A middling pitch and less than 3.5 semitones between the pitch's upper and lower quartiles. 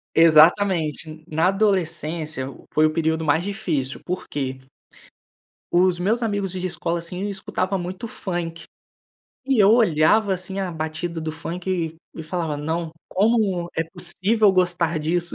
Yes: medium, 175 Hz; average, 3.1 semitones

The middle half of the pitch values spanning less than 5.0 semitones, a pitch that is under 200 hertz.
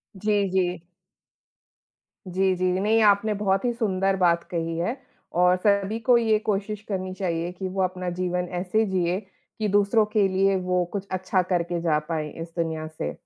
Yes: narrow, 2.4 semitones; high, 190 Hz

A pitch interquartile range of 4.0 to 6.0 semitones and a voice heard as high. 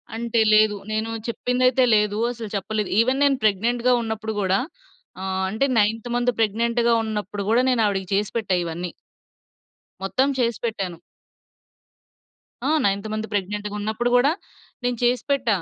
No: average, 2.9 semitones; high, 220 Hz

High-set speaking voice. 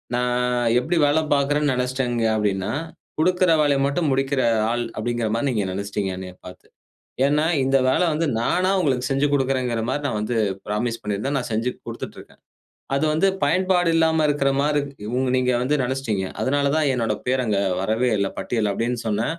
No: low, 130 Hz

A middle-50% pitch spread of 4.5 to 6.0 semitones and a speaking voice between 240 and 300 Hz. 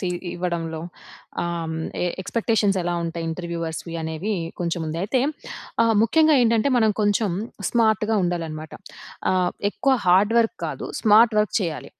No: average, 4.9 semitones; medium, 185 Hz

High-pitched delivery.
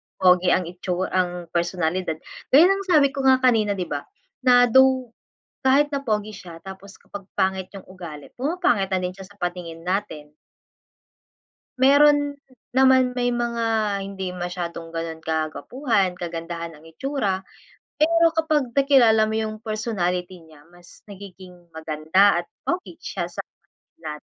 Yes: high, 195 Hz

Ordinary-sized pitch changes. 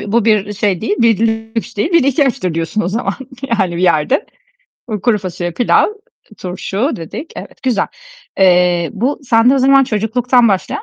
Yes: average, 5.0 semitones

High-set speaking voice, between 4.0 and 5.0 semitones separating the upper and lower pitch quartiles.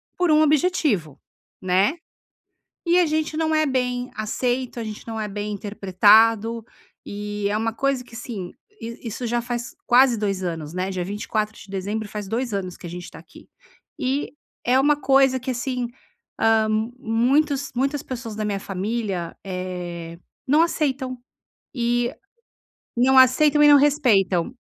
Yes: high, 230 Hz; average, 4.6 semitones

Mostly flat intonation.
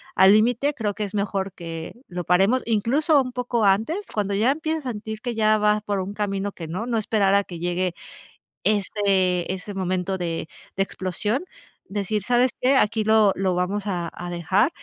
No: average, 3.1 semitones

